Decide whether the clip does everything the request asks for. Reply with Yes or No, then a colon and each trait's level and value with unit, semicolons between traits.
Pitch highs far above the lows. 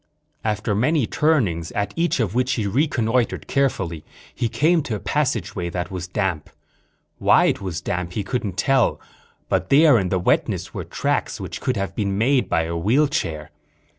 Yes: wide, 6.5 semitones